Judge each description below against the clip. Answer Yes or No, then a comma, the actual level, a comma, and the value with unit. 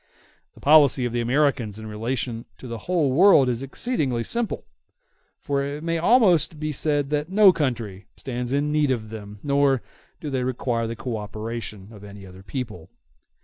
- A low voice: Yes, low, 130 Hz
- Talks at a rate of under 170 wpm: No, average, 175 wpm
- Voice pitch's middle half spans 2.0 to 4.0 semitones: No, average, 4.7 semitones